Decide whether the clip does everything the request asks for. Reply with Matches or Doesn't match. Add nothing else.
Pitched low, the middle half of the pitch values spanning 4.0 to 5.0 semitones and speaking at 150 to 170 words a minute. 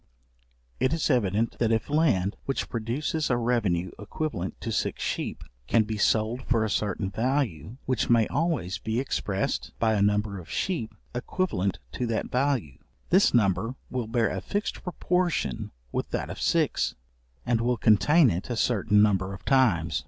Matches